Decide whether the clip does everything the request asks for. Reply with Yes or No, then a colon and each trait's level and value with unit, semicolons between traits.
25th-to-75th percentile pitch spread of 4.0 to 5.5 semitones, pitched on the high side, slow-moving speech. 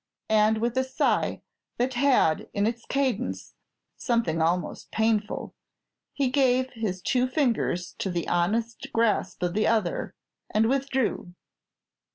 Yes: average, 4.5 semitones; high, 225 Hz; slow, 130 wpm